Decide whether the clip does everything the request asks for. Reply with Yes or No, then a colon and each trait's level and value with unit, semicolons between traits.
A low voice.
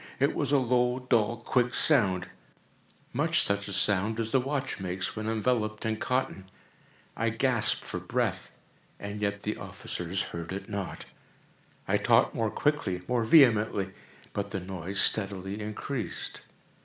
Yes: low, 110 Hz